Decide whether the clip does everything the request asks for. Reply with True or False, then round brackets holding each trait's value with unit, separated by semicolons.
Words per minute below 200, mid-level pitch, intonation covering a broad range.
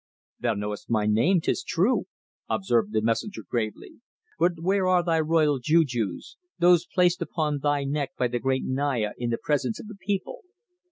True (170 wpm; 145 Hz; 6.9 semitones)